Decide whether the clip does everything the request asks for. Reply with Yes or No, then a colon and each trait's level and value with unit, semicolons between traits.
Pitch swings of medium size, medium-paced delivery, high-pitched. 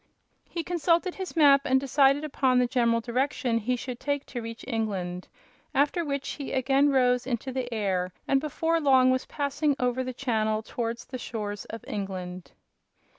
Yes: average, 3.5 semitones; average, 170 wpm; very high, 255 Hz